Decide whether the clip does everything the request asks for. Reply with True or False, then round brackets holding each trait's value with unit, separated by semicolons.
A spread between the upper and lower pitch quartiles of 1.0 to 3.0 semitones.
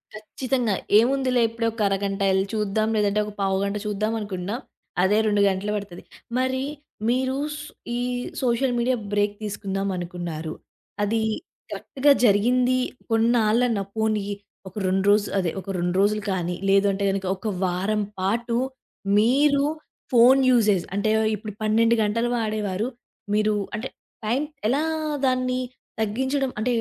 False (3.4 semitones)